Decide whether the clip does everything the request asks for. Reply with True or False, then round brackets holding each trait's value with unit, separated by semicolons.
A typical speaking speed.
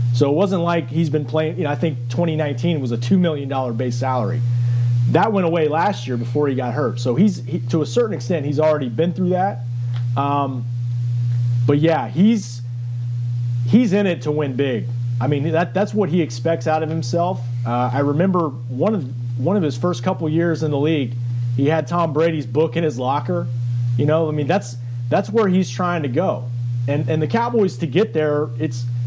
False (210 wpm)